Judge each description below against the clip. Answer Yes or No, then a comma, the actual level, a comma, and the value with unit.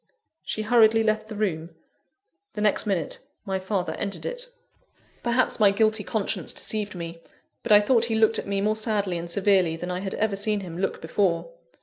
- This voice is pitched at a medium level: No, high, 205 Hz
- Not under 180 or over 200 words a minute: Yes, average, 190 wpm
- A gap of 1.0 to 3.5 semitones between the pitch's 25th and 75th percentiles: Yes, average, 2.7 semitones